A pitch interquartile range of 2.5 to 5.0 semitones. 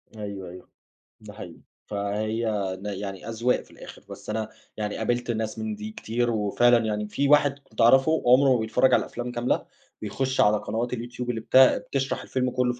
Yes: average, 2.8 semitones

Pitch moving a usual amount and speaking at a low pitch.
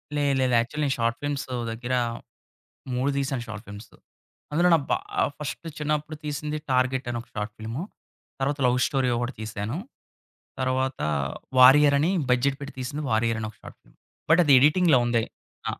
Yes: average, 3.7 semitones; low, 130 Hz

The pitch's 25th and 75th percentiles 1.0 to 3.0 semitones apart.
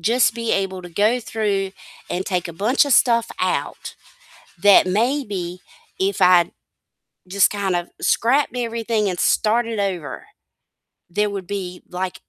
No: average, 3.9 semitones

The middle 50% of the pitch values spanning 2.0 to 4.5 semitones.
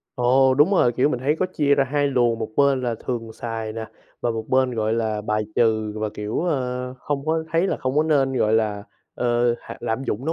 Yes: average, 3.8 semitones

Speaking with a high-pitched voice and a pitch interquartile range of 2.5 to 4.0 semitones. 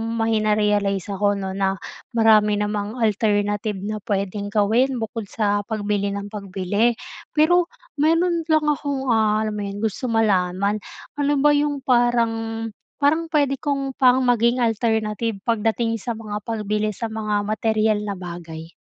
Yes: high, 215 Hz; average, 2.9 semitones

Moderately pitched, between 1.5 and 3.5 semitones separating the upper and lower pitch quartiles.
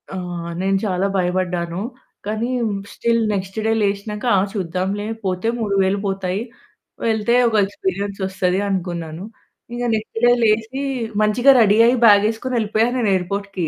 No: high, 200 Hz; average, 2.9 semitones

